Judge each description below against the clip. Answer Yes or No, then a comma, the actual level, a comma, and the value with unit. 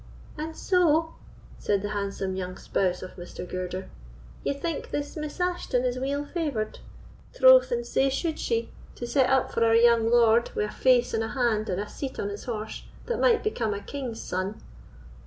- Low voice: No, high, 240 Hz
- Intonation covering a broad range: Yes, wide, 5.9 semitones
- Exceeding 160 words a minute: Yes, average, 190 wpm